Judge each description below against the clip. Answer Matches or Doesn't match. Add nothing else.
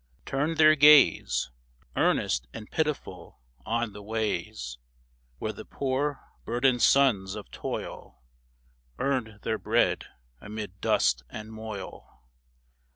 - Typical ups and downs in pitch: Doesn't match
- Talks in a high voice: Doesn't match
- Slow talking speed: Matches